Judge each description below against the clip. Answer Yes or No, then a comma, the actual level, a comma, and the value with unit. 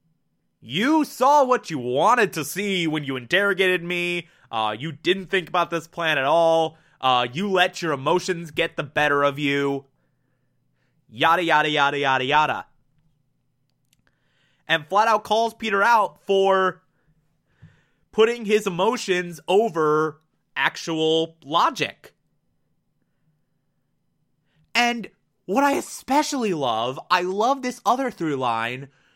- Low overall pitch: No, medium, 165 Hz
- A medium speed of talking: No, slow, 120 wpm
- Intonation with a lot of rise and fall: No, average, 4.6 semitones